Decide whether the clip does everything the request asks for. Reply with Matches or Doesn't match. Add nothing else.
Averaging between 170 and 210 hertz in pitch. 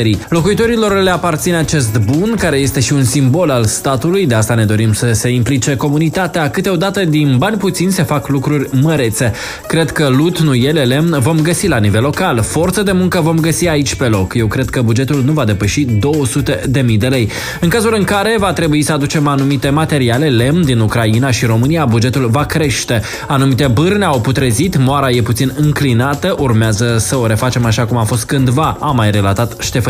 Doesn't match